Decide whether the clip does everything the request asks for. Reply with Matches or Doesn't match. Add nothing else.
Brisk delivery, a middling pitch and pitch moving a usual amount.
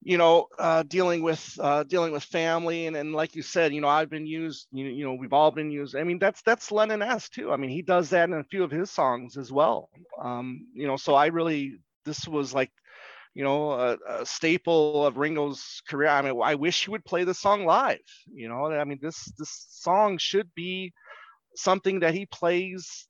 Matches